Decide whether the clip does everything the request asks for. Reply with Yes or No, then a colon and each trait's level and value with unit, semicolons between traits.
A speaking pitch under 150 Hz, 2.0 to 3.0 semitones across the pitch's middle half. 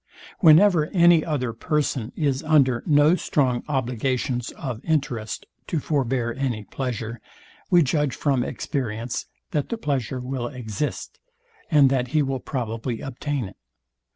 No: low, 135 Hz; average, 3.6 semitones